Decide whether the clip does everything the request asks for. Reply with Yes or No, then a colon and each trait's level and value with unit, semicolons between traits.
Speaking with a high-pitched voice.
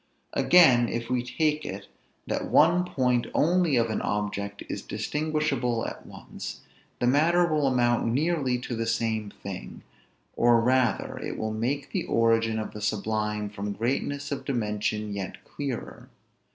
No: low, 120 Hz